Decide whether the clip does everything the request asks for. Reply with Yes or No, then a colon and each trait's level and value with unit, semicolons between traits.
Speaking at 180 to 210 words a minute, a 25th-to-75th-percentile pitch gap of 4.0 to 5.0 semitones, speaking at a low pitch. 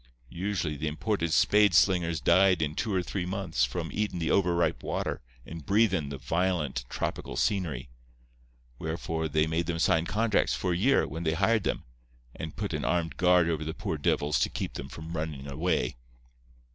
No: average, 185 wpm; average, 3.0 semitones; very low, 85 Hz